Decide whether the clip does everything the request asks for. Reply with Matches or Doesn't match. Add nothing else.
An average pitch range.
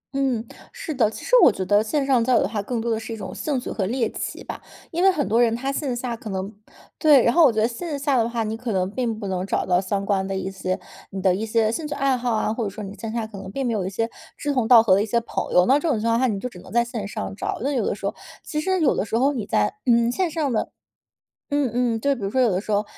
Matches